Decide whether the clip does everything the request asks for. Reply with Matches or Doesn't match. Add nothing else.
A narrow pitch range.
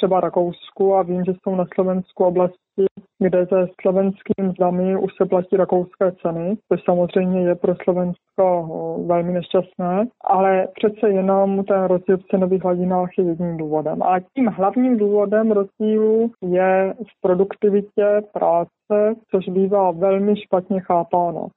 Matches